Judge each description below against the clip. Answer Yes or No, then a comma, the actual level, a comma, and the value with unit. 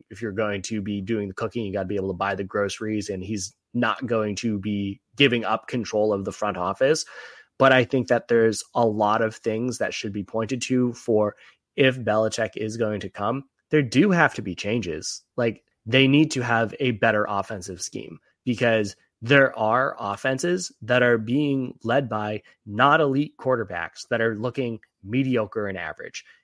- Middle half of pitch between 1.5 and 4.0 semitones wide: Yes, average, 3.3 semitones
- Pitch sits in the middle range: No, low, 115 Hz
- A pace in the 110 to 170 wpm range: No, average, 190 wpm